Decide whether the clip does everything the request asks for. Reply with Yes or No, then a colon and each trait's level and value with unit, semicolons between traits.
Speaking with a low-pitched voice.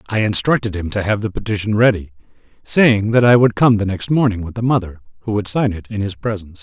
Yes: low, 105 Hz